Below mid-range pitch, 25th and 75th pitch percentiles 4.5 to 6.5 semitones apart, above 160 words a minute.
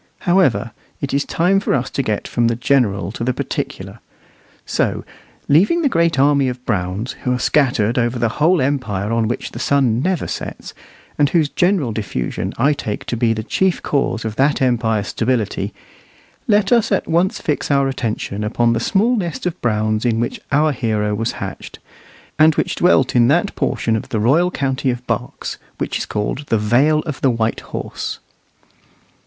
Yes: low, 125 Hz; average, 5.0 semitones; average, 180 wpm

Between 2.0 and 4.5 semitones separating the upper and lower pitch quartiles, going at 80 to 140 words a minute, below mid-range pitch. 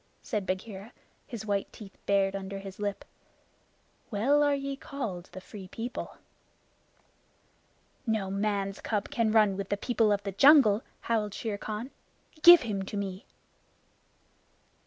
No: average, 2.8 semitones; slow, 135 wpm; high, 210 Hz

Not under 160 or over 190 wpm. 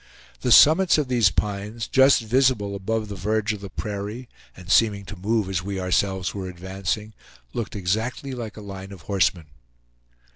Yes: average, 170 wpm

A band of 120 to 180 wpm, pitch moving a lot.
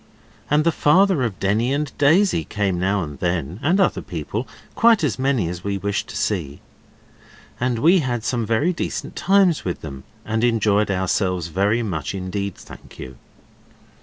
Yes: average, 165 wpm; wide, 7.8 semitones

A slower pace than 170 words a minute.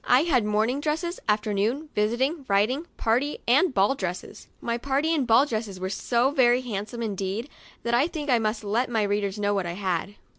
No: average, 190 wpm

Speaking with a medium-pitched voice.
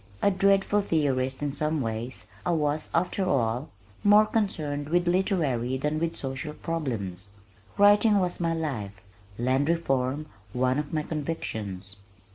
Yes: medium, 150 Hz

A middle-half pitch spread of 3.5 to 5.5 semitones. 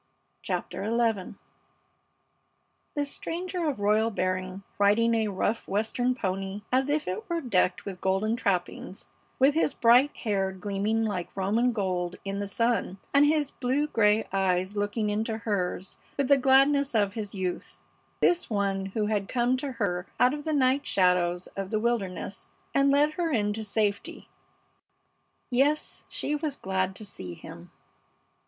Yes: average, 5.0 semitones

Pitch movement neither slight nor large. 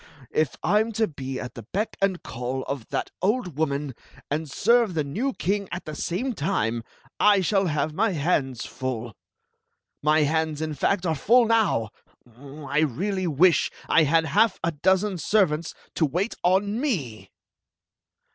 No: wide, 6.0 semitones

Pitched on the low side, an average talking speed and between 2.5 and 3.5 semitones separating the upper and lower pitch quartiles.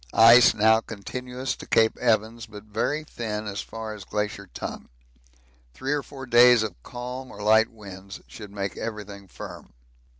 Yes: low, 110 Hz; average, 160 wpm; average, 2.9 semitones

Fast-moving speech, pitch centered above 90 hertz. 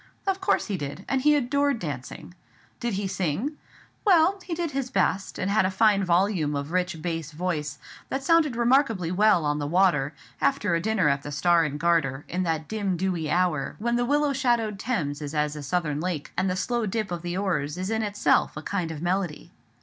Yes: fast, 210 wpm; medium, 185 Hz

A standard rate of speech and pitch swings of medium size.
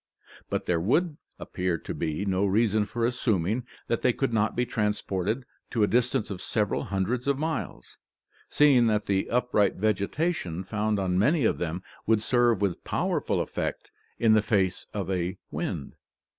Yes: average, 165 wpm; average, 4.2 semitones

